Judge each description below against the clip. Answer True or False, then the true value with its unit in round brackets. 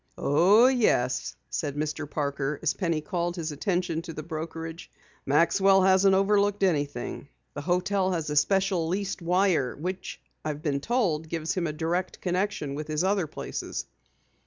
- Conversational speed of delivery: True (155 wpm)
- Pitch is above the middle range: False (170 Hz)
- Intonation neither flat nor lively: True (3.9 semitones)